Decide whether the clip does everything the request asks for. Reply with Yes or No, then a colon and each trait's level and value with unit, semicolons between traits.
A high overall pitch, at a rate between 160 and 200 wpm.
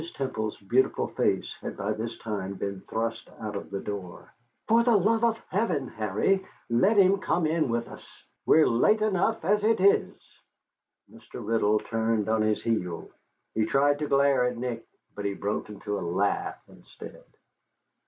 No: low, 115 Hz; average, 165 wpm